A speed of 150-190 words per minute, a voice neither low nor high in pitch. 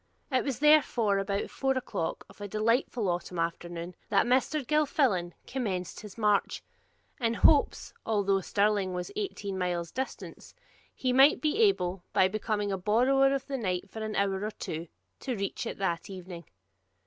No: average, 160 wpm; high, 210 Hz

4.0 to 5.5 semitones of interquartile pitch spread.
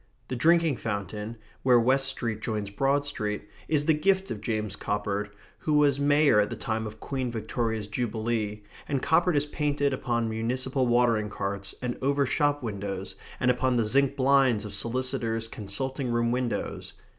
Yes: average, 4.4 semitones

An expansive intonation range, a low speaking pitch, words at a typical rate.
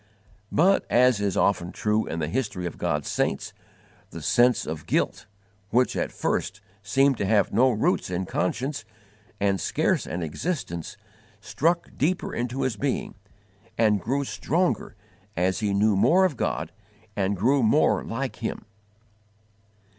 Yes: wide, 5.7 semitones; low, 110 Hz; average, 145 wpm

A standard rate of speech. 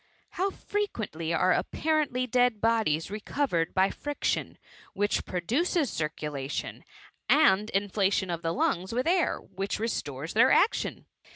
No: slow, 120 wpm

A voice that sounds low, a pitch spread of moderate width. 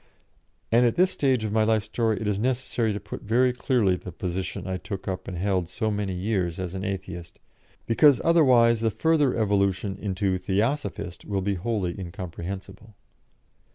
Yes: low, 100 Hz; average, 3.7 semitones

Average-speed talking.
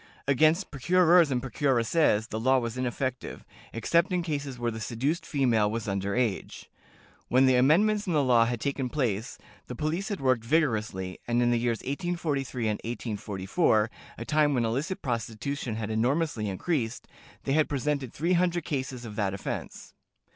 Yes: average, 165 wpm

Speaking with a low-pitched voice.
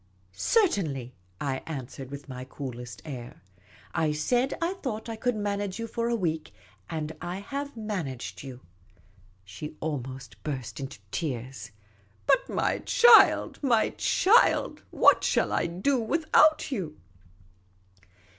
No: medium, 160 Hz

